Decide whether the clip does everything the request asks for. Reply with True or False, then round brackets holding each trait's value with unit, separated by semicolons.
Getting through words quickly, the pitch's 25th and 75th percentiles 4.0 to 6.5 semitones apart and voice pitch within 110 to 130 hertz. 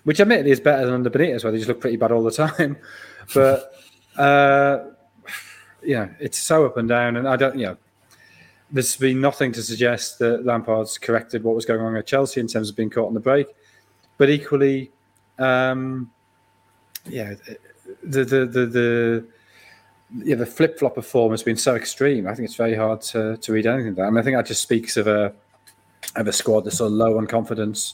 False (215 wpm; 3.3 semitones; 120 Hz)